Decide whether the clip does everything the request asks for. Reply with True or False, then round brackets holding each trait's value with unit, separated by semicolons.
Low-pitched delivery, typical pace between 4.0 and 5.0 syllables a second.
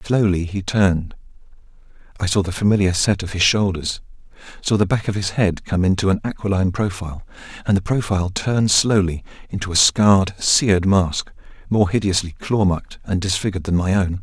False (95 Hz; 5.6 syllables/s)